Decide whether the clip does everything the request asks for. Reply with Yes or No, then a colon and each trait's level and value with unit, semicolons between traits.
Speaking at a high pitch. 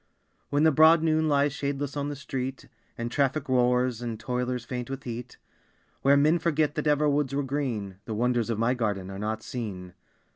No: low, 130 Hz